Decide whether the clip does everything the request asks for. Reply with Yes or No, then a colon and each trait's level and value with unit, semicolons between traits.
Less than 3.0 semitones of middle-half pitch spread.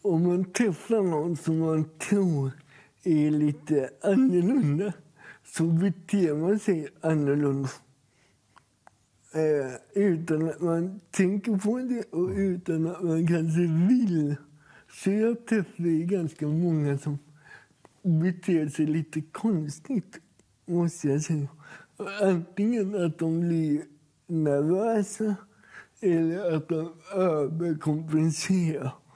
No: average, 4.0 semitones